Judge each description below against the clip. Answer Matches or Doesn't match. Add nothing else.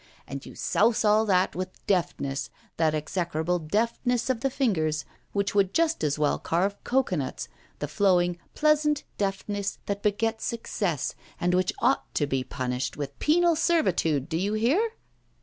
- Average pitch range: Doesn't match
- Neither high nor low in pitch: Doesn't match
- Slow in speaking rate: Doesn't match